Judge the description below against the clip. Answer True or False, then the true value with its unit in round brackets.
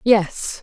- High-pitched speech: True (205 Hz)